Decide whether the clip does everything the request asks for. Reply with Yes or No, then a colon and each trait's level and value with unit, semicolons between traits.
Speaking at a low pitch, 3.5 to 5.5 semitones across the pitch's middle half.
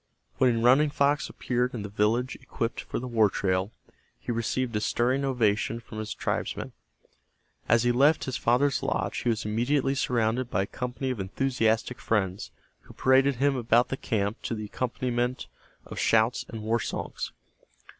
No: low, 120 Hz; average, 2.8 semitones